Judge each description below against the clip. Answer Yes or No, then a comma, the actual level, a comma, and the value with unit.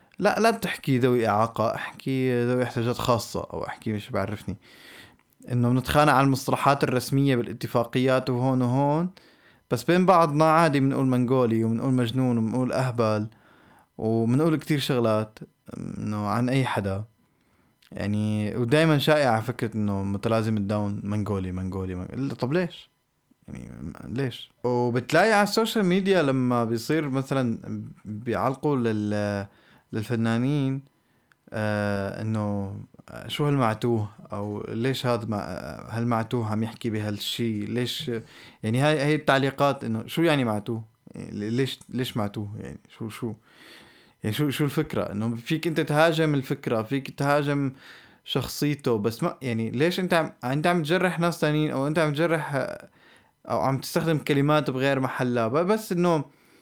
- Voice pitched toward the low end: Yes, low, 125 Hz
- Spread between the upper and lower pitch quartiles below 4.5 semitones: No, average, 4.8 semitones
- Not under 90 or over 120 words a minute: No, average, 130 wpm